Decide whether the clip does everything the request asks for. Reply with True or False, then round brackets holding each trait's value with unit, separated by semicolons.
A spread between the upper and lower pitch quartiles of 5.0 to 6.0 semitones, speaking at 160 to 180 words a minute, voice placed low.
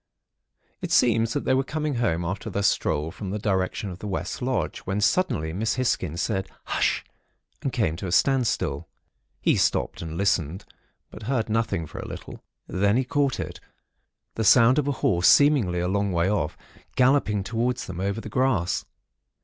True (5.4 semitones; 175 wpm; 105 Hz)